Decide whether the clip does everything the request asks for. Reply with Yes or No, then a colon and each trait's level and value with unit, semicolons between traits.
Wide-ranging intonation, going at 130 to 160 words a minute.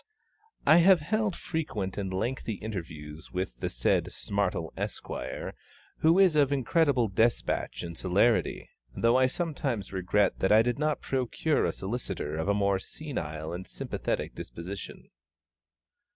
Yes: wide, 7.7 semitones; slow, 135 wpm